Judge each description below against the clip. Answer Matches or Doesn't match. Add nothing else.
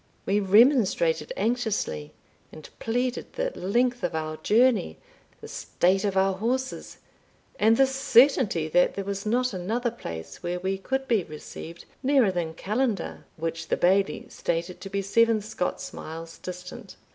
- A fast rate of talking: Doesn't match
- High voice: Matches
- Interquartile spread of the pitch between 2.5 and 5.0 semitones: Doesn't match